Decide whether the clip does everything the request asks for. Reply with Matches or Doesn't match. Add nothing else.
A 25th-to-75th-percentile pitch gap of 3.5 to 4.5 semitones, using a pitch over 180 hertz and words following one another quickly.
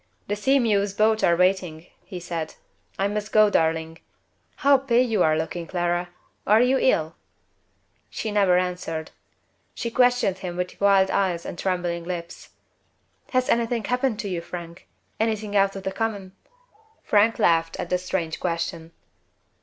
Doesn't match